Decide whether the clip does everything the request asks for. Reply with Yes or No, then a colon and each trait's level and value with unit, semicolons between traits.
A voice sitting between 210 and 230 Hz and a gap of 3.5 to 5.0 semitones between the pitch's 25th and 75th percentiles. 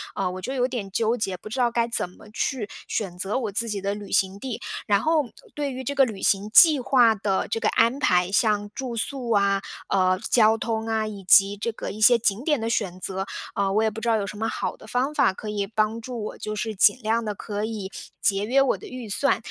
No: high, 215 Hz; average, 3.1 semitones